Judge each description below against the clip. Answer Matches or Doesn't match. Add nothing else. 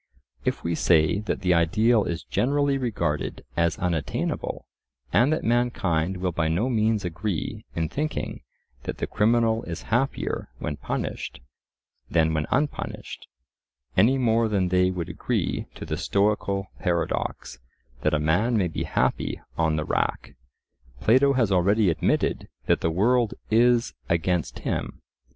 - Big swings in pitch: Matches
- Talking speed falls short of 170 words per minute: Matches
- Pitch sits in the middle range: Doesn't match